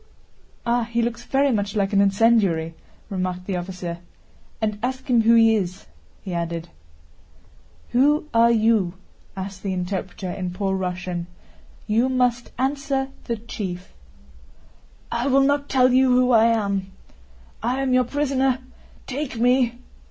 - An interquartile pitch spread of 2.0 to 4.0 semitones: No, average, 5.0 semitones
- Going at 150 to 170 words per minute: No, slow, 135 wpm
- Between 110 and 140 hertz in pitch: No, high, 230 Hz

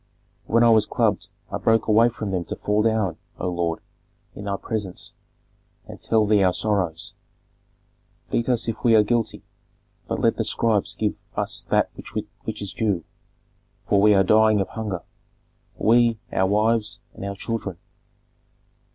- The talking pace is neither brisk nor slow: Yes, average, 160 wpm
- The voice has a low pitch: Yes, low, 105 Hz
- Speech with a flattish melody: Yes, narrow, 2.3 semitones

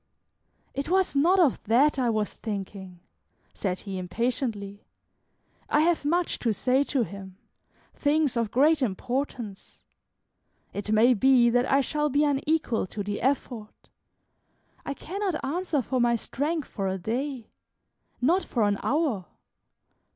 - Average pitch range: No, wide, 5.7 semitones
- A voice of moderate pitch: No, very high, 255 Hz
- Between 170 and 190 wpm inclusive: No, slow, 135 wpm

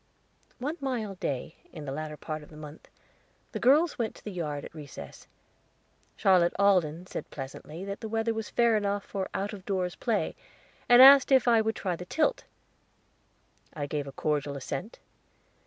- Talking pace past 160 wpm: Yes, average, 175 wpm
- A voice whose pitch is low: No, high, 190 Hz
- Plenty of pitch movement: Yes, wide, 6.6 semitones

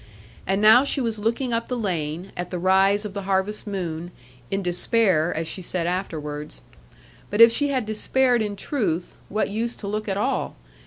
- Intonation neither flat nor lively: Yes, average, 4.1 semitones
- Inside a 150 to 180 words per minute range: No, average, 190 wpm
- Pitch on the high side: Yes, high, 200 Hz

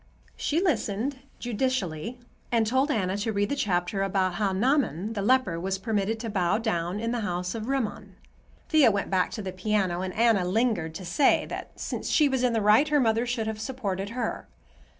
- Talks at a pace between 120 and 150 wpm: No, average, 195 wpm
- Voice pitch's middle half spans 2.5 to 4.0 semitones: No, average, 4.4 semitones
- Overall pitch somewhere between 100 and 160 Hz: No, high, 215 Hz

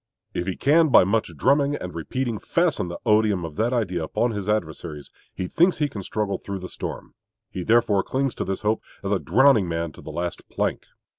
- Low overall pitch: Yes, low, 105 Hz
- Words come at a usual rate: No, fast, 210 wpm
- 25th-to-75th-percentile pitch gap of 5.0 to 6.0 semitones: Yes, wide, 5.6 semitones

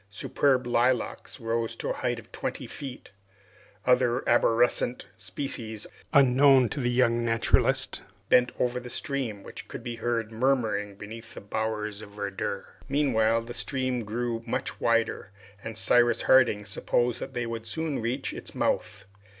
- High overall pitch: No, low, 120 Hz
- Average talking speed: Yes, average, 150 wpm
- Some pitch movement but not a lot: No, narrow, 2.2 semitones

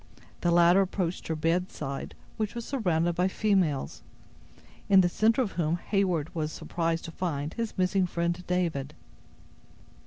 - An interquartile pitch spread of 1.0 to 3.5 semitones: Yes, average, 2.7 semitones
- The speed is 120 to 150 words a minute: Yes, average, 145 wpm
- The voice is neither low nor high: Yes, medium, 175 Hz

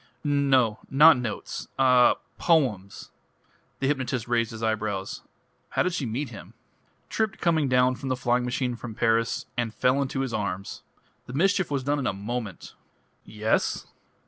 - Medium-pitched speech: No, low, 125 Hz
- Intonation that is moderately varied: Yes, average, 3.6 semitones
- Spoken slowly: No, average, 155 wpm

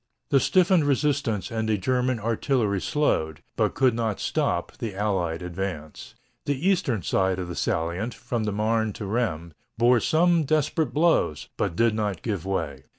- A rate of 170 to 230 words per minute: No, average, 160 wpm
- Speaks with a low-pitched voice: Yes, low, 110 Hz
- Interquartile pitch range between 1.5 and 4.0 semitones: No, wide, 5.6 semitones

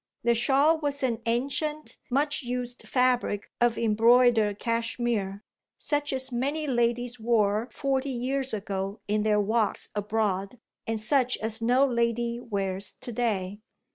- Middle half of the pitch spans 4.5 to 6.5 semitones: No, average, 3.2 semitones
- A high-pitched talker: Yes, high, 235 Hz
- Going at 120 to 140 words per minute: Yes, slow, 135 wpm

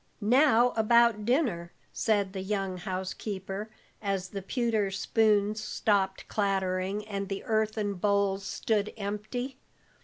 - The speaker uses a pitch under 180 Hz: No, high, 205 Hz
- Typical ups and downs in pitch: No, narrow, 2.2 semitones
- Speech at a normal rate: No, slow, 115 wpm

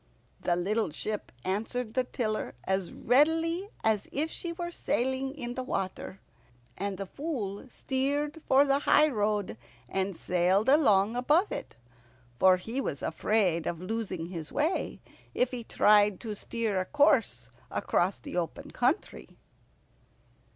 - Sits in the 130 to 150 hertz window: No, high, 220 Hz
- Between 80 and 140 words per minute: Yes, slow, 135 wpm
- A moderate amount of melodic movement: No, wide, 6.2 semitones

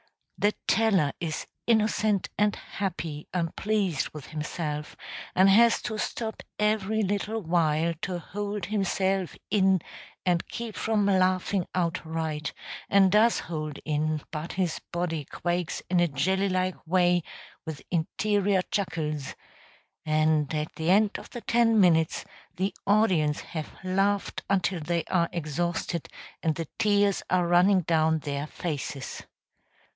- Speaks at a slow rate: Yes, slow, 130 wpm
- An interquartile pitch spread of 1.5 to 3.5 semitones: No, average, 4.1 semitones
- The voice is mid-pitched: Yes, medium, 180 Hz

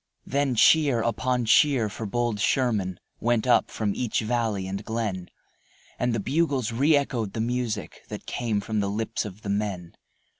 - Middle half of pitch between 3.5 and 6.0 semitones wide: No, average, 3.1 semitones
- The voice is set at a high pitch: No, low, 115 Hz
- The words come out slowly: No, average, 165 wpm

